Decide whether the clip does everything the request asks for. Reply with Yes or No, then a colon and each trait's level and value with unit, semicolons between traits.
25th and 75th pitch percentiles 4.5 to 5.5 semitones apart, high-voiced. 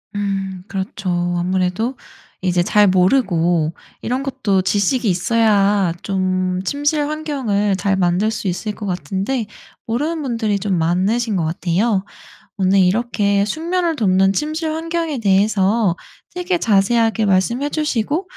Yes: average, 5.1 semitones; high, 205 Hz